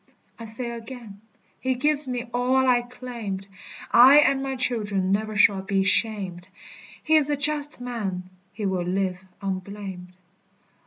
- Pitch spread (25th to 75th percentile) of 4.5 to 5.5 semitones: Yes, average, 4.9 semitones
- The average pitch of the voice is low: No, high, 225 Hz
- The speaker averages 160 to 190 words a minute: No, average, 145 wpm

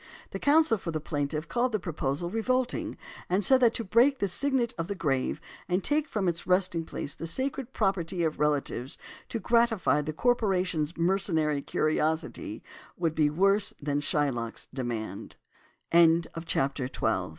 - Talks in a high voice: No, medium, 180 Hz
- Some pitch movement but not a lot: No, wide, 6.8 semitones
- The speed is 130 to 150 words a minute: Yes, average, 140 wpm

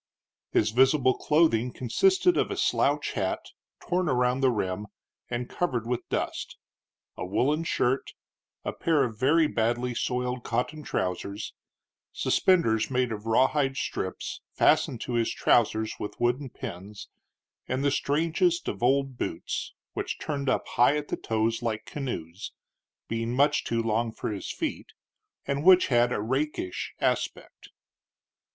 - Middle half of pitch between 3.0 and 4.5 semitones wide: Yes, average, 4.0 semitones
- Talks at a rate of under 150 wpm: Yes, average, 140 wpm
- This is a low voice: Yes, low, 125 Hz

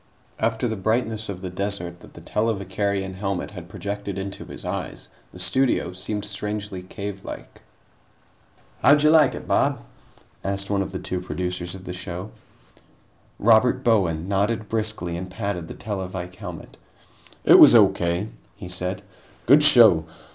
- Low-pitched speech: Yes, low, 100 Hz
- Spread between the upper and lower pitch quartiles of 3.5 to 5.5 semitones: No, average, 3.1 semitones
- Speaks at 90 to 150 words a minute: Yes, average, 145 wpm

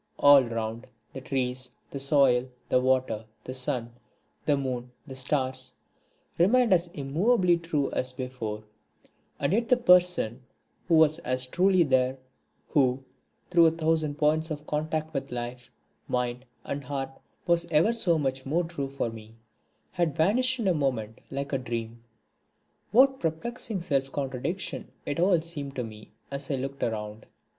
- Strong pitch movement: No, average, 4.7 semitones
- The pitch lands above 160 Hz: No, medium, 140 Hz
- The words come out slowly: No, average, 150 wpm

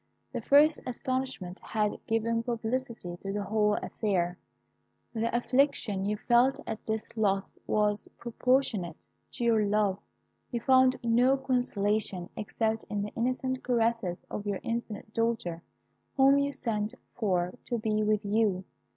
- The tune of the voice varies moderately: Yes, average, 3.1 semitones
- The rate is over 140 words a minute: No, slow, 135 wpm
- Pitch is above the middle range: Yes, high, 220 Hz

